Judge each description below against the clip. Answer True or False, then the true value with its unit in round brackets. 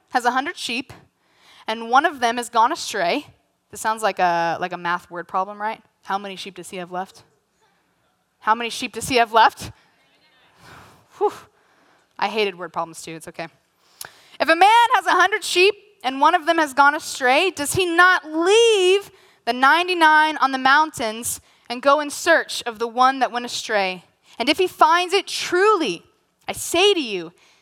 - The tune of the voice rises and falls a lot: True (8.6 semitones)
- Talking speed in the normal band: True (190 wpm)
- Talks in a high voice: True (255 Hz)